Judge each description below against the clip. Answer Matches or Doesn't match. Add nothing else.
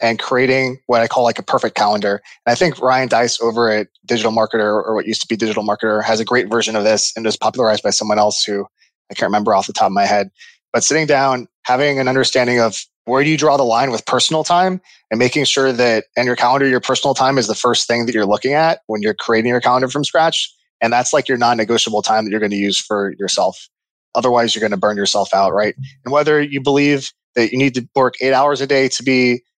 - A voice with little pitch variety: Doesn't match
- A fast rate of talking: Matches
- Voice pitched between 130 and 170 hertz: Doesn't match